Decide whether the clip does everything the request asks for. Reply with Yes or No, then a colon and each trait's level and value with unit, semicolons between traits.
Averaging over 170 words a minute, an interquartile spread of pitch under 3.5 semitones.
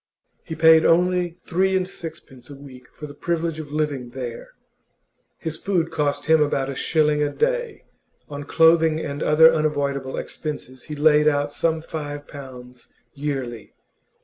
No: average, 150 wpm; narrow, 2.4 semitones